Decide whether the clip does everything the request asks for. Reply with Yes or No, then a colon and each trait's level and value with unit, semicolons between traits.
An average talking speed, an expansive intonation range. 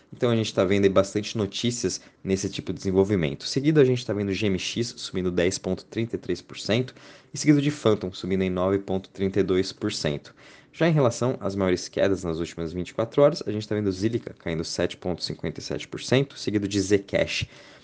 No: average, 160 wpm; average, 4.0 semitones